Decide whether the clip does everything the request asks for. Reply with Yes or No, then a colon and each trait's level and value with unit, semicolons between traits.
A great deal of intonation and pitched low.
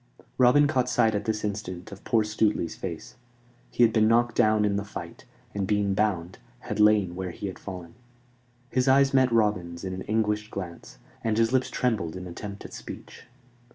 No: average, 3.2 semitones; low, 105 Hz